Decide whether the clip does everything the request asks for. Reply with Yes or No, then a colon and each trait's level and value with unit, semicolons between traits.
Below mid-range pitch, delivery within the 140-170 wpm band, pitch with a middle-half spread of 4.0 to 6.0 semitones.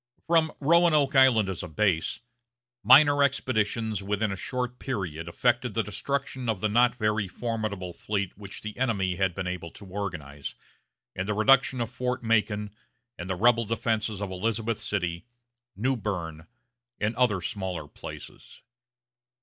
Yes: low, 105 Hz; average, 150 wpm; average, 4.5 semitones